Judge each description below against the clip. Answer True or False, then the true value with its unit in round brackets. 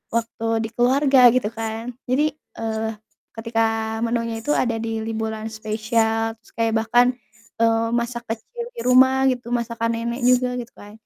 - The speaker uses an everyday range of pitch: False (1.6 semitones)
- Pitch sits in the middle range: False (230 Hz)